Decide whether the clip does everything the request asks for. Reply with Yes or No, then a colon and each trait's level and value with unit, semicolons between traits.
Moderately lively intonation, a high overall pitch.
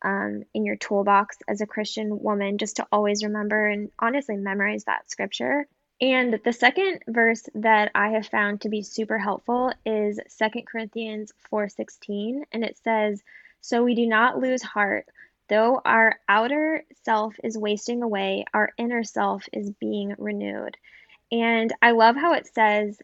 No: narrow, 2.2 semitones; high, 215 Hz